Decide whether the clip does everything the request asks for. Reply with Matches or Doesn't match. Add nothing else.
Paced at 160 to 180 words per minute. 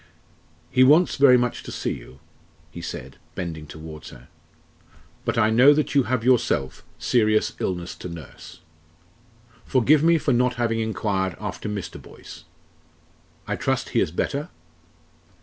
Doesn't match